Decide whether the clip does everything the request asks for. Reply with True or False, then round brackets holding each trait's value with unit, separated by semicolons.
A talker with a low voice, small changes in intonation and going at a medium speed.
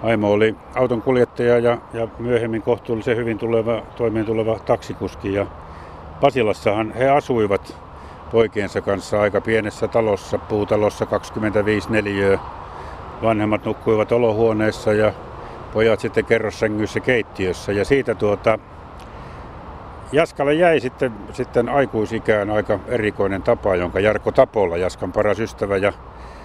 True (110 Hz; 2.1 semitones; 115 wpm)